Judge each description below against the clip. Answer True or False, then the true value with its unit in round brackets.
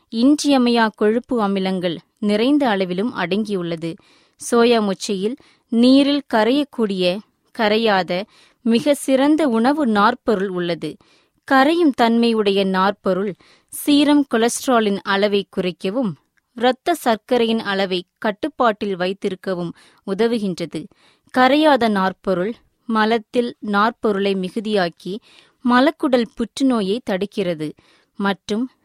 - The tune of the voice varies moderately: True (4.3 semitones)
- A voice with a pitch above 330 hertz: False (220 Hz)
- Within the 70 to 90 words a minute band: True (80 wpm)